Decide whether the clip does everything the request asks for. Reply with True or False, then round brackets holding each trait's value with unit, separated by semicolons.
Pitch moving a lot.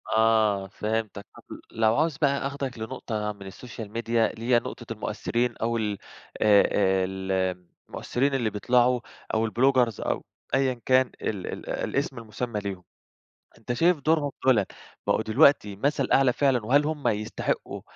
False (3.8 semitones)